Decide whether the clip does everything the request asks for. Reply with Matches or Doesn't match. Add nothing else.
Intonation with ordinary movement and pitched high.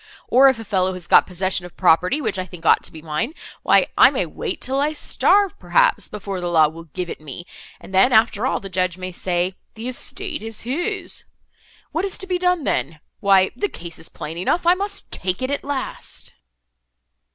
Doesn't match